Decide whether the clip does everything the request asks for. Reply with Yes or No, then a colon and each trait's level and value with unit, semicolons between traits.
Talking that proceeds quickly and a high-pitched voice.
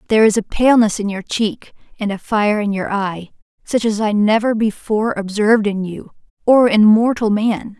No: average, 190 wpm; high, 215 Hz